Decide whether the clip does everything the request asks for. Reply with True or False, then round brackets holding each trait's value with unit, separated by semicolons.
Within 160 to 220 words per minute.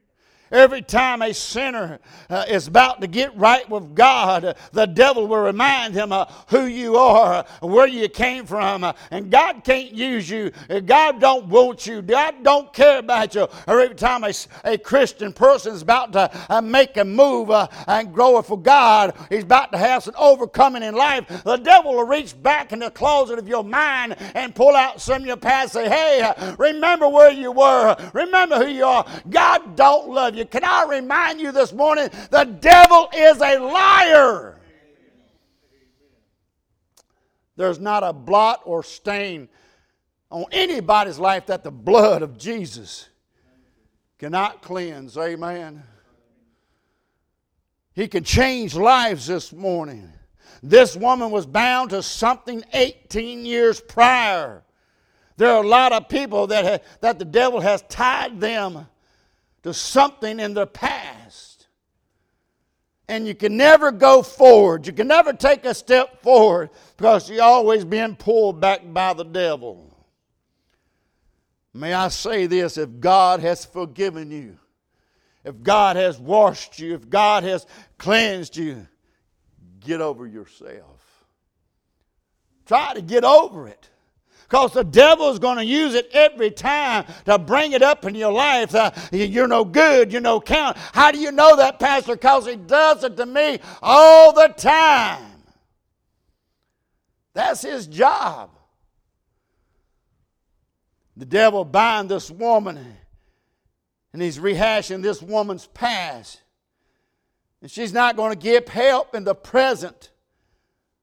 False (150 wpm)